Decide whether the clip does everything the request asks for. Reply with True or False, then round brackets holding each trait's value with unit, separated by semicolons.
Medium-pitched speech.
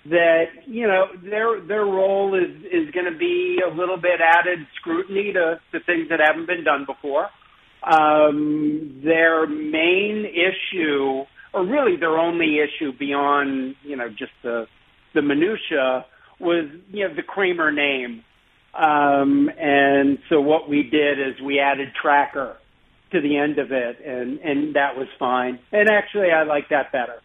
True (155 Hz)